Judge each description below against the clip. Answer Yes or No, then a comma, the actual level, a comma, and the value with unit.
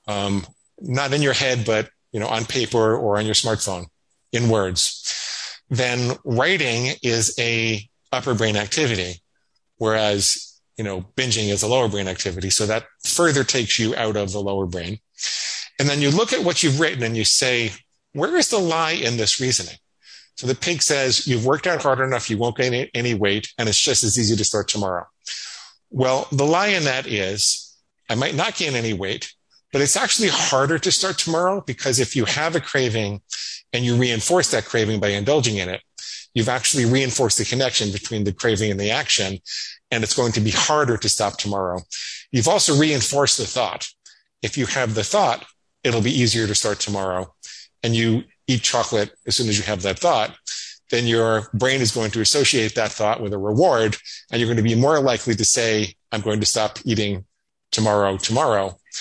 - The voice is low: Yes, low, 115 Hz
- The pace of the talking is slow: No, average, 195 wpm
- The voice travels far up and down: No, average, 3.9 semitones